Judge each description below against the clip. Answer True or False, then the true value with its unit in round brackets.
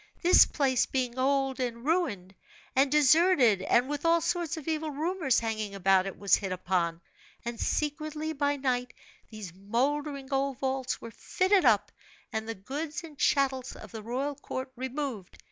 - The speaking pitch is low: False (265 Hz)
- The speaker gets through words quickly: False (160 wpm)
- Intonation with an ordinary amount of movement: True (4.7 semitones)